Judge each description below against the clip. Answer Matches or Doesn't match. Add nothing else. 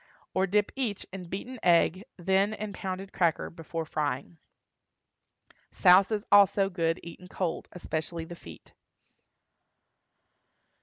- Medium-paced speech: Doesn't match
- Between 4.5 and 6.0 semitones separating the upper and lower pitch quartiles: Doesn't match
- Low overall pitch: Doesn't match